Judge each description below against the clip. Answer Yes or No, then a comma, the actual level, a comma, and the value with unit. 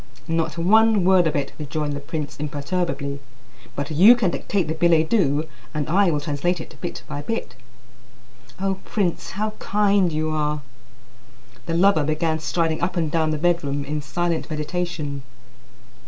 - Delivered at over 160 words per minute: No, average, 155 wpm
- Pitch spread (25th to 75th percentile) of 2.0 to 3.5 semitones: Yes, average, 3.1 semitones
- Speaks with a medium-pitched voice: Yes, medium, 160 Hz